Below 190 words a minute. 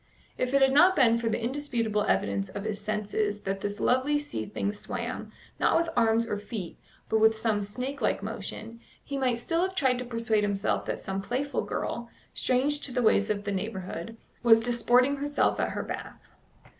No: average, 195 wpm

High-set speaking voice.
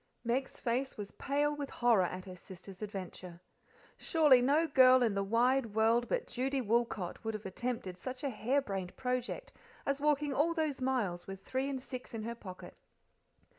Yes: high, 245 Hz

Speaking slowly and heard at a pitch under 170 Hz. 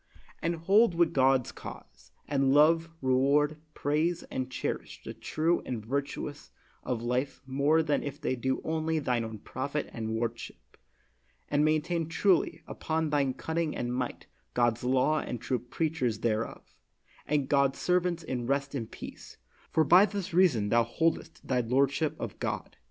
No: average, 155 wpm; medium, 140 Hz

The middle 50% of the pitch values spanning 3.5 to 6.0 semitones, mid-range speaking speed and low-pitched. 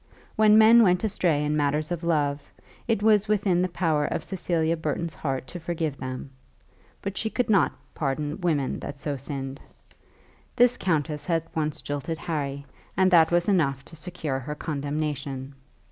No: average, 4.0 semitones; average, 160 wpm; medium, 160 Hz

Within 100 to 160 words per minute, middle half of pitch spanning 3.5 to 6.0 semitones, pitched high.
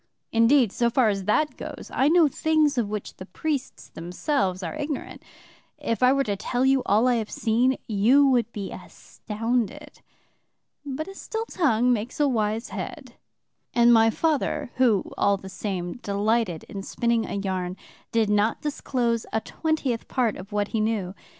No: average, 170 wpm; average, 4.4 semitones; high, 230 Hz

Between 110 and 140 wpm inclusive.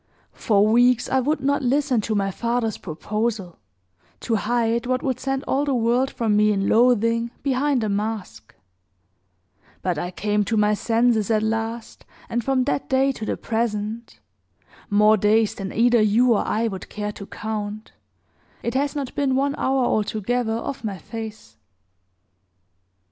No: average, 160 wpm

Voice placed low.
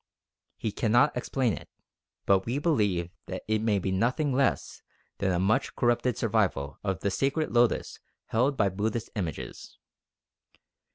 Yes: low, 110 Hz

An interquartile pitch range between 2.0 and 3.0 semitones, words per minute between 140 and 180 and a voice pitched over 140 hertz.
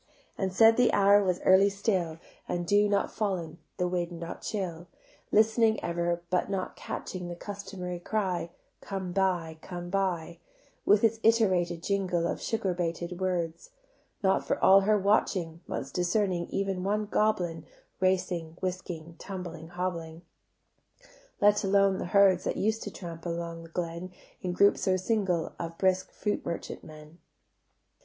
Yes: narrow, 2.6 semitones; average, 150 wpm; medium, 185 Hz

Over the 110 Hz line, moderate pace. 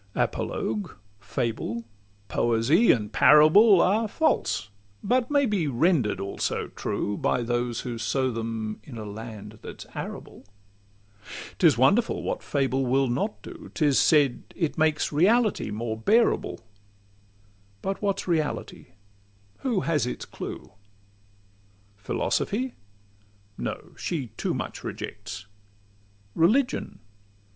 No: low, 135 Hz; slow, 115 wpm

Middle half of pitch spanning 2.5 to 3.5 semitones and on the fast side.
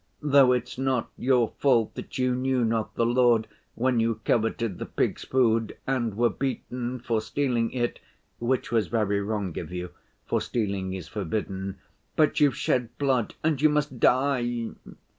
No: average, 2.8 semitones; average, 160 wpm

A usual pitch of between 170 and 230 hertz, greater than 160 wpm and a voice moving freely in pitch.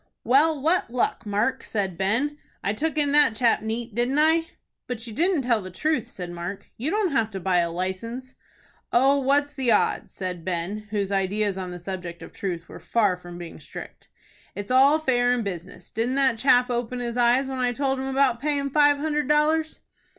No: high, 240 Hz; average, 200 wpm; wide, 6.0 semitones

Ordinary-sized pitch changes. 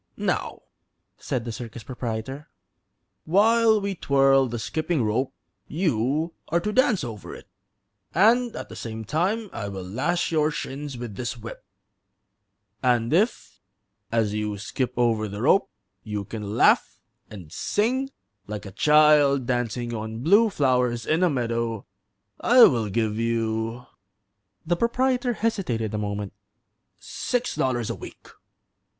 No: wide, 7.5 semitones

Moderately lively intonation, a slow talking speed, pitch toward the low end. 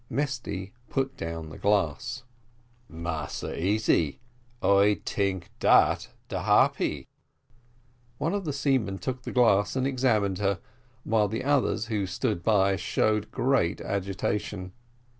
Yes: average, 4.9 semitones; slow, 120 wpm; low, 105 Hz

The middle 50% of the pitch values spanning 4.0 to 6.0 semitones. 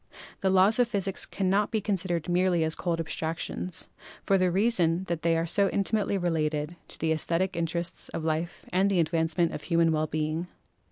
No: average, 2.7 semitones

